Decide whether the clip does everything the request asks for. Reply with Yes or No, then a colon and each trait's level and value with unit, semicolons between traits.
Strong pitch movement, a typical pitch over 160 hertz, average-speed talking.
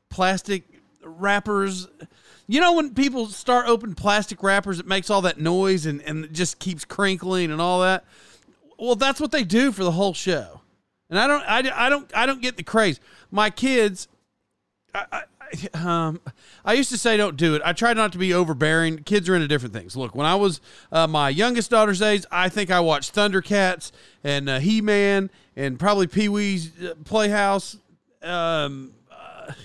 No: average, 4.3 semitones; high, 190 Hz; average, 180 wpm